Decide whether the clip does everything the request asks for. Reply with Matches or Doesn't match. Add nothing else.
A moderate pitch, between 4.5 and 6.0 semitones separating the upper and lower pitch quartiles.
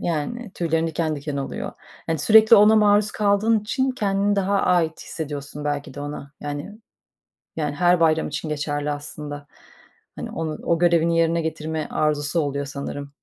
Matches